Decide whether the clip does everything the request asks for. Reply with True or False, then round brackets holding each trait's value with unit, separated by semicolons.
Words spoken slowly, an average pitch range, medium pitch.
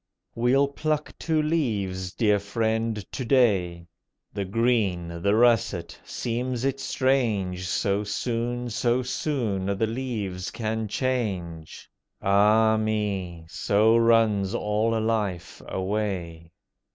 False (105 wpm; 3.9 semitones; 110 Hz)